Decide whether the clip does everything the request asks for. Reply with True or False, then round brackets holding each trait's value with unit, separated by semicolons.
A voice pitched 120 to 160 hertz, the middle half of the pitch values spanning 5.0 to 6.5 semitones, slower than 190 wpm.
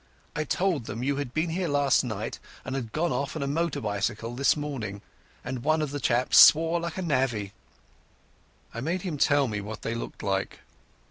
False (140 Hz; 5.3 semitones; 200 wpm)